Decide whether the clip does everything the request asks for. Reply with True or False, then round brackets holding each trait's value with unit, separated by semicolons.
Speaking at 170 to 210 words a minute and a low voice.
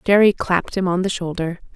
False (205 wpm; 185 Hz)